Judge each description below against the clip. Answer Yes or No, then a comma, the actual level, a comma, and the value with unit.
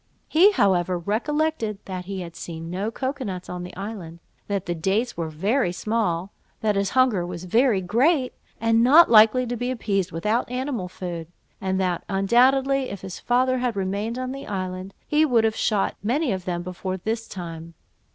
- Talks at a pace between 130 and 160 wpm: No, average, 180 wpm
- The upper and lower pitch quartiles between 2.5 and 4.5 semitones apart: No, wide, 5.4 semitones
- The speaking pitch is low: No, high, 205 Hz